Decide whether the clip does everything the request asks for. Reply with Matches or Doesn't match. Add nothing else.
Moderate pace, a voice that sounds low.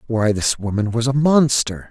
Matches